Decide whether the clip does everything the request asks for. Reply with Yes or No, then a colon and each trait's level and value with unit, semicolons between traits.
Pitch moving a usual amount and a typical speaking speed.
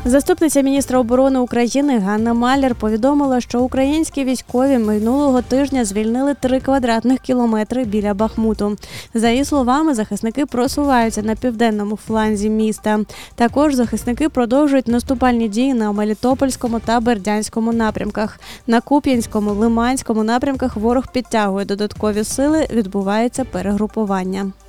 Yes: average, 3.4 semitones; average, 115 wpm